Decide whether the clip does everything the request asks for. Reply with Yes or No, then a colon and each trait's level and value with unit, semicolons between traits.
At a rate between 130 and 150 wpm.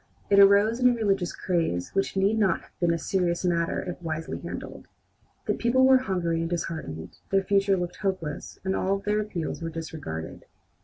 No: average, 185 wpm